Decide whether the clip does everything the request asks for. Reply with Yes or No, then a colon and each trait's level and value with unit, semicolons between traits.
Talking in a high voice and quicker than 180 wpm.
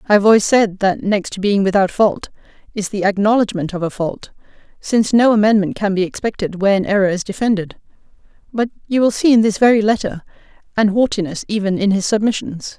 Yes: high, 205 Hz; average, 190 wpm